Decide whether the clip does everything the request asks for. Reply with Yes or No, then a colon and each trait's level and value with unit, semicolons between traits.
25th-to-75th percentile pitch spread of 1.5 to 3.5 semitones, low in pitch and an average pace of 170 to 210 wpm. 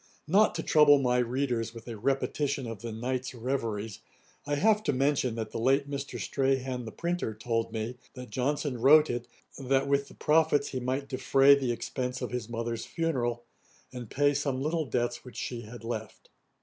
Yes: average, 3.1 semitones; low, 130 Hz; average, 185 wpm